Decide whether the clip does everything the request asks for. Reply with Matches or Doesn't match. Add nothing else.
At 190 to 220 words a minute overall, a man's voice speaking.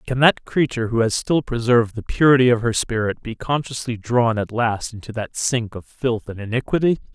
Matches